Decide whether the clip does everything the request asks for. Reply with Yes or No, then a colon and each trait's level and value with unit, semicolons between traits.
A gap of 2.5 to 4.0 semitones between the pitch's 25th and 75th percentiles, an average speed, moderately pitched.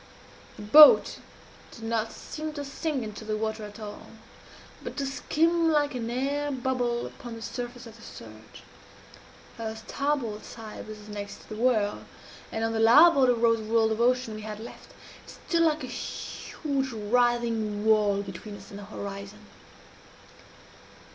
No: average, 3.6 semitones; average, 160 wpm; high, 230 Hz